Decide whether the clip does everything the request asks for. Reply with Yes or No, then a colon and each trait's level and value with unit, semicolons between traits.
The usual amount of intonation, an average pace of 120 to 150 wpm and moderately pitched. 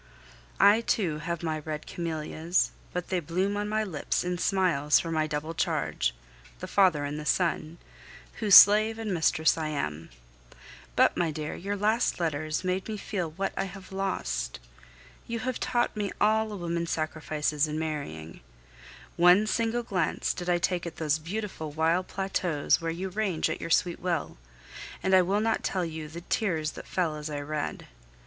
No: average, 4.0 semitones; average, 175 wpm; medium, 170 Hz